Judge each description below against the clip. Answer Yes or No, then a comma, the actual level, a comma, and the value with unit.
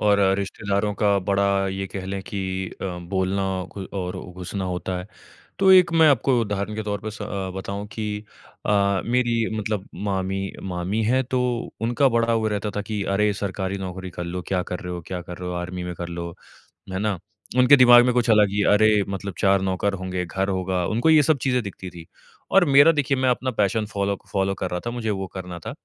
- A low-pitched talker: Yes, low, 100 Hz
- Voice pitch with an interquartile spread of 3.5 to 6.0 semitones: No, average, 3.1 semitones